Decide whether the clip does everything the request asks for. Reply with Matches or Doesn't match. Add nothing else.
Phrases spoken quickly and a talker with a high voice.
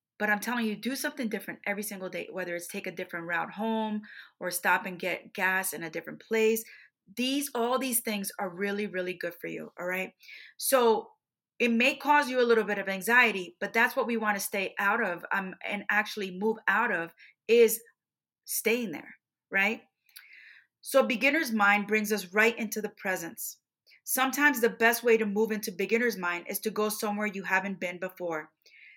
Doesn't match